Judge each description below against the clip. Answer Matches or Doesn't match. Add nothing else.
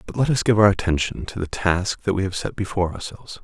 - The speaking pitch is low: Matches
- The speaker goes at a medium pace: Doesn't match